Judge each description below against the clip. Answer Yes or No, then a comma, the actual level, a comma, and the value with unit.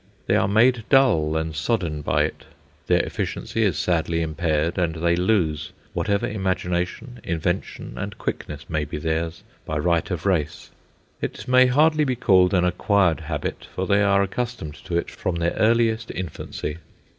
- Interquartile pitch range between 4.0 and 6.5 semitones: Yes, average, 5.1 semitones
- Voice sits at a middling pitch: No, very low, 90 Hz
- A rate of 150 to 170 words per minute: Yes, average, 160 wpm